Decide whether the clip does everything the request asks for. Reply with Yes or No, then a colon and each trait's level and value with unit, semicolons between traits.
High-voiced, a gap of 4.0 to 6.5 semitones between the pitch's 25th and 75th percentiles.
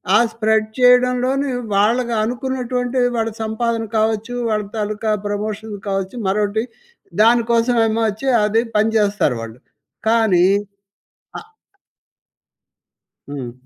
No: high, 220 Hz; narrow, 2.6 semitones